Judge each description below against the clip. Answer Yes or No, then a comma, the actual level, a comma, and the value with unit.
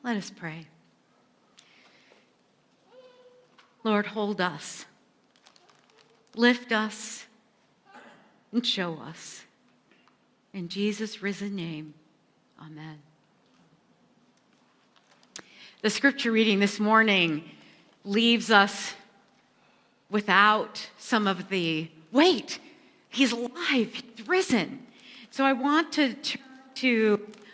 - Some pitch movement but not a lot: Yes, average, 3.8 semitones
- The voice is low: No, high, 215 Hz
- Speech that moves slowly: Yes, slow, 85 wpm